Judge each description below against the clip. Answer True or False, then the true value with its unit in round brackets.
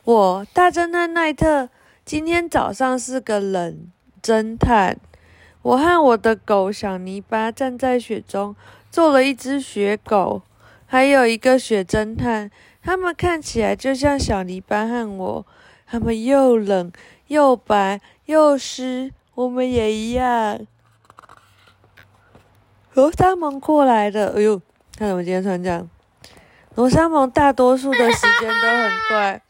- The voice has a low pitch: False (230 Hz)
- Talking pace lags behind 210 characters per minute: True (185 characters per minute)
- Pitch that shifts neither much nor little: True (5.0 semitones)